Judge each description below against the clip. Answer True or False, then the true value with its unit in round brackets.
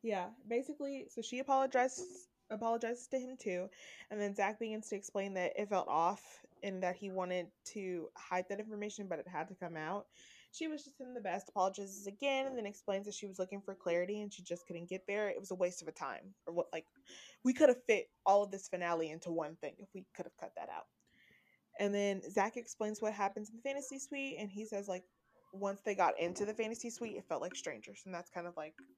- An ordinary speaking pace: False (235 wpm)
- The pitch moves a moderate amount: True (3.9 semitones)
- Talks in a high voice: True (200 Hz)